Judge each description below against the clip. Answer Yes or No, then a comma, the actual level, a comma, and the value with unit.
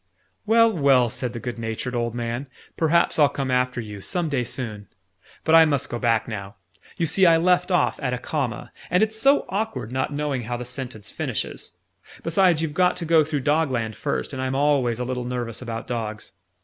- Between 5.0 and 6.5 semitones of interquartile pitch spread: Yes, average, 5.3 semitones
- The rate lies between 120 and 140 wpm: No, average, 200 wpm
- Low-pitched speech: Yes, low, 130 Hz